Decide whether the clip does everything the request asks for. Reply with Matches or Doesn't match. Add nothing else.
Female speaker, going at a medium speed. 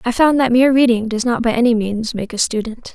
Doesn't match